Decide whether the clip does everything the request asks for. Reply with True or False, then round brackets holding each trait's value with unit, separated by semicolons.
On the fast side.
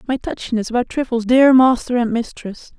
False (170 wpm)